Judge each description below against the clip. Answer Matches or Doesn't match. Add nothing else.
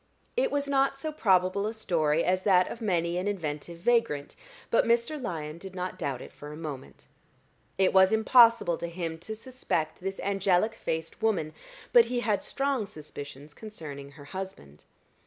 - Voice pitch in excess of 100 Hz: Matches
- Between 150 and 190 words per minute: Matches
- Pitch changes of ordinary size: Doesn't match